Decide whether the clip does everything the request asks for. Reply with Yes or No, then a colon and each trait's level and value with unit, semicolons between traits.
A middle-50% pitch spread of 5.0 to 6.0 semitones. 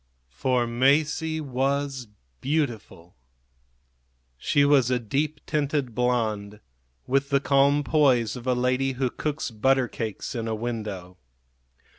No: average, 3.6 semitones